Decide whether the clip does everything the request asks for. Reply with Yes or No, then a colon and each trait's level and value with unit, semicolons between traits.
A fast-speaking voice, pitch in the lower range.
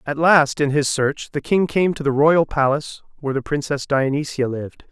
No: fast, 210 wpm; medium, 145 Hz